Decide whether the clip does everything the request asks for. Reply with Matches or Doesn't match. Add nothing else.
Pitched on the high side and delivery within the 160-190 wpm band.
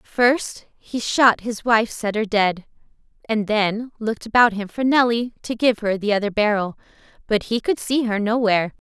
Matches